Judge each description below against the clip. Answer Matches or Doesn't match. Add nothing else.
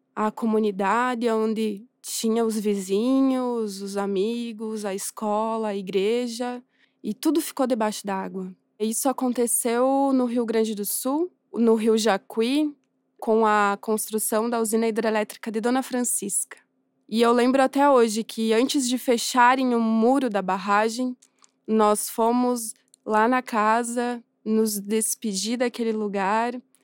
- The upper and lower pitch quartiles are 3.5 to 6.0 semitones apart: Doesn't match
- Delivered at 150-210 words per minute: Doesn't match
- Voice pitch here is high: Matches